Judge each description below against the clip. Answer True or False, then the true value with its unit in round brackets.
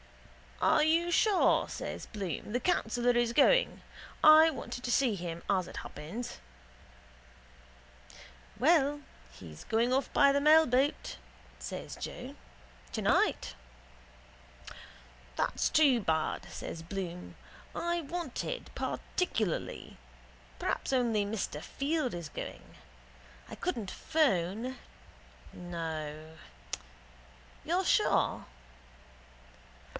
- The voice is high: True (240 Hz)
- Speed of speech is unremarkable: False (95 wpm)